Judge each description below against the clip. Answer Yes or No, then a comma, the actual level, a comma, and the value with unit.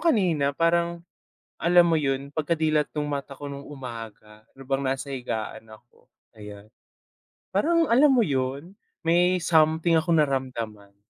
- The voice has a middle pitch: Yes, medium, 145 Hz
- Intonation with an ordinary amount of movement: Yes, average, 4.4 semitones